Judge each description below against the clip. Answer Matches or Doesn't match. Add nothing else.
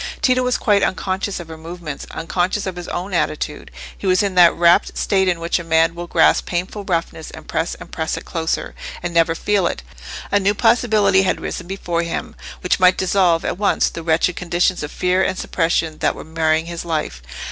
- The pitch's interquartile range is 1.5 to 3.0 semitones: Matches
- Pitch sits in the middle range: Matches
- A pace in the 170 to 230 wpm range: Matches